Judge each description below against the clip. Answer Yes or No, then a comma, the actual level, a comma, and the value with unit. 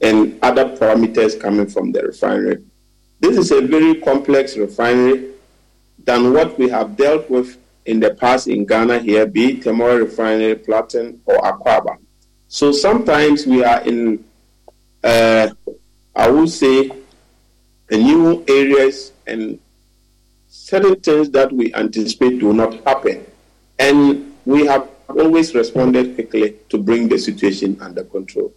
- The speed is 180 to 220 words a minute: No, slow, 135 wpm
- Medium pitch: No, low, 125 Hz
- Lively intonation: No, average, 3.8 semitones